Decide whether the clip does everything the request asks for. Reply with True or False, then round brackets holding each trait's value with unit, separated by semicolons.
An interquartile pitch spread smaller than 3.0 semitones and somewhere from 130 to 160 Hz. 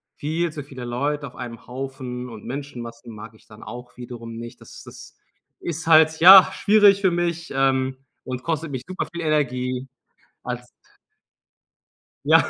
False (4.6 semitones; 135 Hz)